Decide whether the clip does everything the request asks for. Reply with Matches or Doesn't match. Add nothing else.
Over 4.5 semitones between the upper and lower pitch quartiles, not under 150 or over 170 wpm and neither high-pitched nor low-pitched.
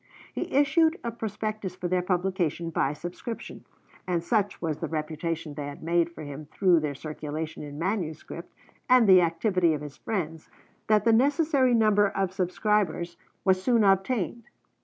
Matches